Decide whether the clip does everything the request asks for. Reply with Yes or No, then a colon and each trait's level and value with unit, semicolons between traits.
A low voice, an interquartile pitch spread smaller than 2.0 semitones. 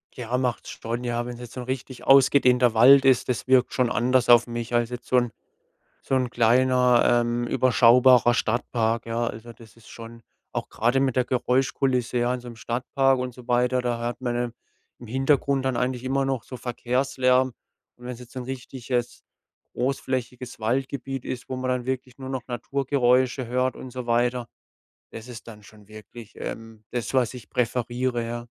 Yes: low, 125 Hz; narrow, 1.5 semitones